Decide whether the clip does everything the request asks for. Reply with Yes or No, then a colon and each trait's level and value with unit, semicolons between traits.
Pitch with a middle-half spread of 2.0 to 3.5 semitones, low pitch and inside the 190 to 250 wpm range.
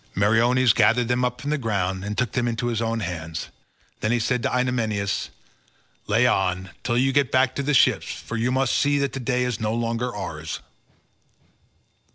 Yes: average, 2.8 semitones; low, 120 Hz; average, 195 wpm